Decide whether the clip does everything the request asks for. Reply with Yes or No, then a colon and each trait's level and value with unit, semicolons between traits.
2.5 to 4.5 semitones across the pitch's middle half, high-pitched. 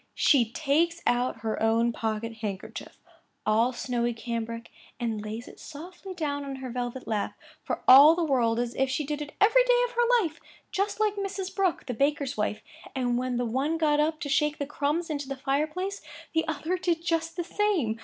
No: wide, 5.6 semitones; very high, 280 Hz